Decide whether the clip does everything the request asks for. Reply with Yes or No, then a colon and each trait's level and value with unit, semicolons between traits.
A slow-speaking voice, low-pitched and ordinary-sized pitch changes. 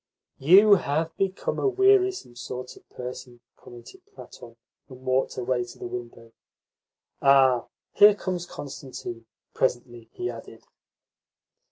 No: slow, 120 wpm; low, 130 Hz; wide, 8.0 semitones